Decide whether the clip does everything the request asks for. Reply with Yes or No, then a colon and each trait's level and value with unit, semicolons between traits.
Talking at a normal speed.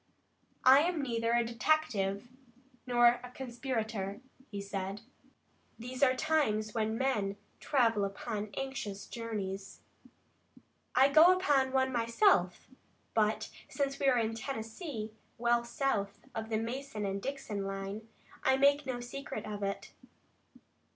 No: slow, 125 wpm